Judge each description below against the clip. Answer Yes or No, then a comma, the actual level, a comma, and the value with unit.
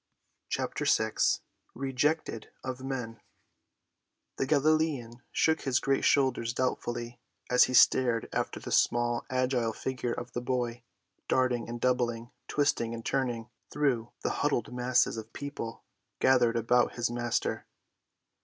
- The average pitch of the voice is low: Yes, low, 125 Hz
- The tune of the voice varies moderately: No, narrow, 2.0 semitones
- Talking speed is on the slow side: Yes, slow, 125 wpm